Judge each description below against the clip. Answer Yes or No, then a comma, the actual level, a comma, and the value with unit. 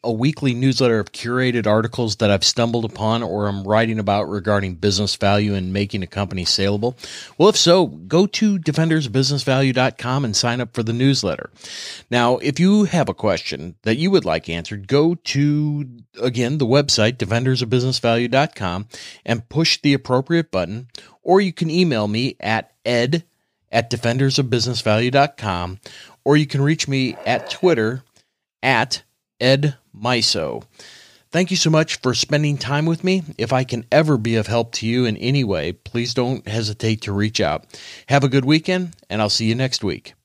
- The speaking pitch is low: Yes, low, 125 Hz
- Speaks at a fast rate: No, average, 165 wpm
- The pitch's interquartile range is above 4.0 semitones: Yes, average, 4.7 semitones